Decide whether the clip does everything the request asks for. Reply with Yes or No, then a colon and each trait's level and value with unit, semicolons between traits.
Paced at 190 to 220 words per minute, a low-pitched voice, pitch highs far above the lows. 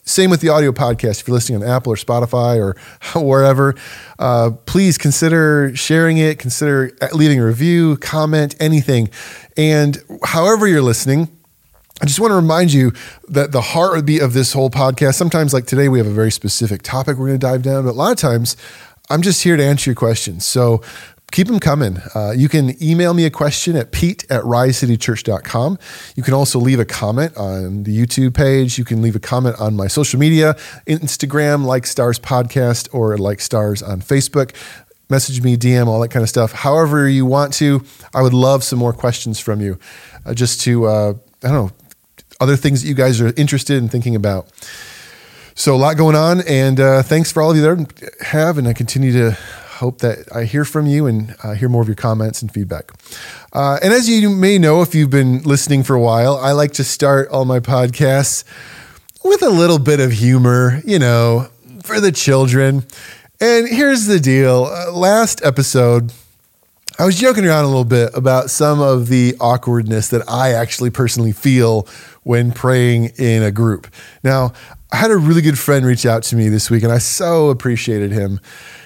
No: average, 200 wpm; low, 130 Hz; average, 4.0 semitones